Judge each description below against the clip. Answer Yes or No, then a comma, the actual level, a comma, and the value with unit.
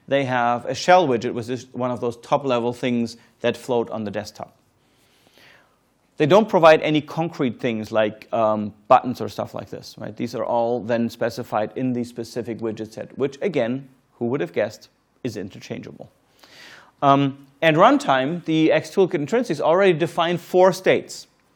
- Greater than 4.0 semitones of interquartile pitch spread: Yes, average, 4.6 semitones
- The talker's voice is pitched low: Yes, low, 125 Hz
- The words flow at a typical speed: Yes, average, 165 wpm